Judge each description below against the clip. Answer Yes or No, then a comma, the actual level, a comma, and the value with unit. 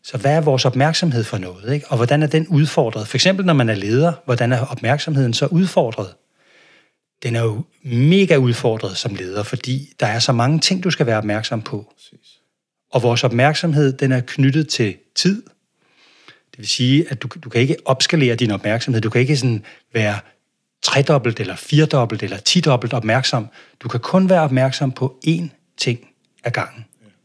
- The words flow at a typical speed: Yes, average, 180 wpm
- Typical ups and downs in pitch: Yes, average, 4.4 semitones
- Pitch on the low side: Yes, low, 130 Hz